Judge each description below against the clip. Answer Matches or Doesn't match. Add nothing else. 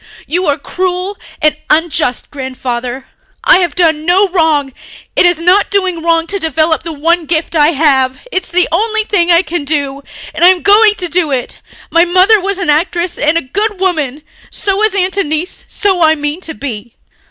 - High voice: Matches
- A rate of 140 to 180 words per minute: Doesn't match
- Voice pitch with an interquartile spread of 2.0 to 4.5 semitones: Matches